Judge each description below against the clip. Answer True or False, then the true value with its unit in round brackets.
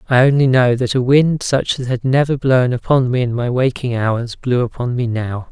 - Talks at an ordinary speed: False (230 wpm)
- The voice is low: True (125 Hz)